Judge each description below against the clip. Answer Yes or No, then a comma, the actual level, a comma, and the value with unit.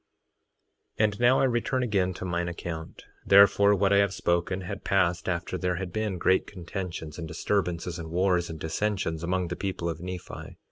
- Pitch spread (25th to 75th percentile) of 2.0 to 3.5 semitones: Yes, average, 2.7 semitones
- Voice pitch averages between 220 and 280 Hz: No, very low, 90 Hz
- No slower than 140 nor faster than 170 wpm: No, average, 185 wpm